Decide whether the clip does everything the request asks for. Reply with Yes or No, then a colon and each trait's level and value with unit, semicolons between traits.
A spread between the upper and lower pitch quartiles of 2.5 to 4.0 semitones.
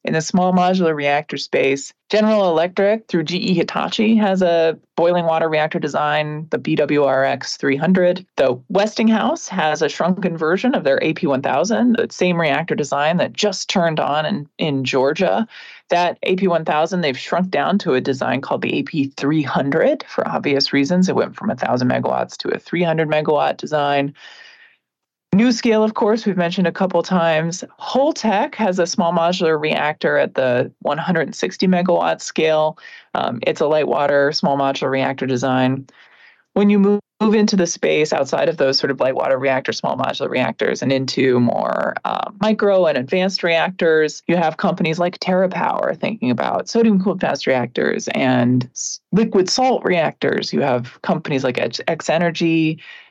No: average, 5.1 semitones